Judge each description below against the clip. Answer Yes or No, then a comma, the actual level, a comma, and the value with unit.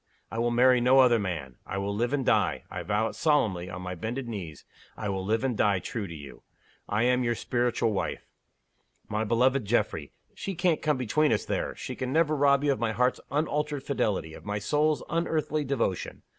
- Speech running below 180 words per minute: No, fast, 205 wpm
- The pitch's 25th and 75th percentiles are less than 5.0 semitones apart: No, average, 5.3 semitones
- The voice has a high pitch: No, low, 120 Hz